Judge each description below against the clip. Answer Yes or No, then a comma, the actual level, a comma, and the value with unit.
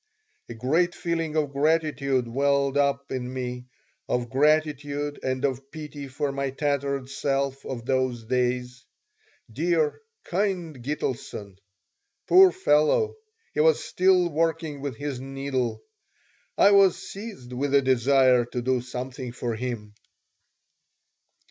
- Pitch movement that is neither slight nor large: Yes, average, 3.2 semitones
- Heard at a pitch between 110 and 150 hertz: Yes, medium, 140 Hz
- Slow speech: Yes, slow, 125 wpm